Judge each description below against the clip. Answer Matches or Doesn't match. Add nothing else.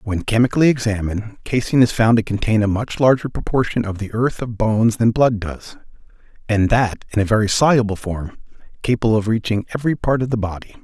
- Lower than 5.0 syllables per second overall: Doesn't match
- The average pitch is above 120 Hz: Doesn't match